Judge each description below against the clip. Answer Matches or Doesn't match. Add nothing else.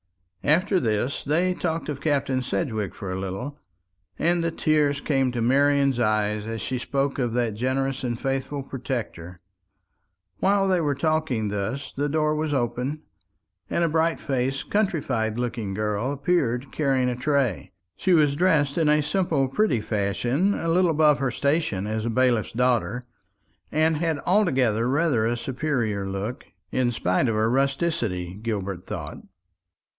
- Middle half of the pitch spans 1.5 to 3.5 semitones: Doesn't match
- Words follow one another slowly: Doesn't match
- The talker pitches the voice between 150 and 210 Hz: Doesn't match